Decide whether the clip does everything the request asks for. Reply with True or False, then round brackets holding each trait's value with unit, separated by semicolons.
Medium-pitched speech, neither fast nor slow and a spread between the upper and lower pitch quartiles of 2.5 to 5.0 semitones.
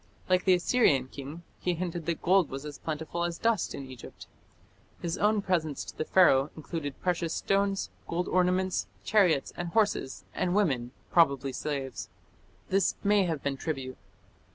True (170 Hz; 155 wpm; 4.6 semitones)